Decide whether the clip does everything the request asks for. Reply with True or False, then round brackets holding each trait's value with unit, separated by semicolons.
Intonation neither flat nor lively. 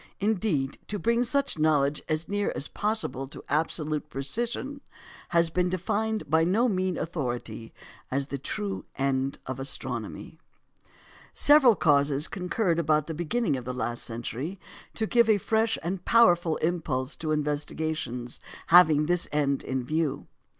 False (6.2 semitones)